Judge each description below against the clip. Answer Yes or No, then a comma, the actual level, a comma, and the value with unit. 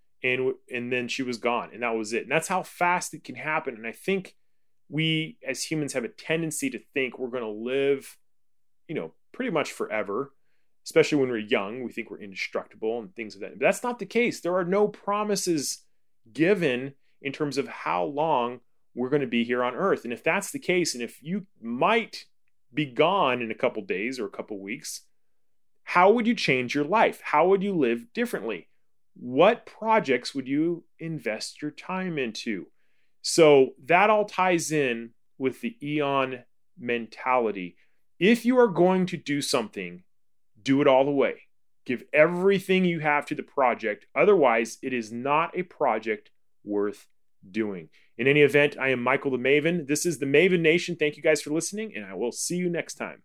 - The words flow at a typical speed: Yes, average, 195 wpm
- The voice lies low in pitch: No, medium, 150 Hz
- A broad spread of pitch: Yes, wide, 6.2 semitones